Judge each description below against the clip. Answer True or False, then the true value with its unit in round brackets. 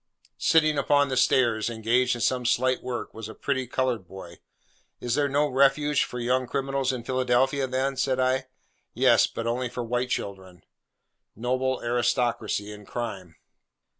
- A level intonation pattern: True (2.1 semitones)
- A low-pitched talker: True (125 Hz)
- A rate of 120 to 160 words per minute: True (155 wpm)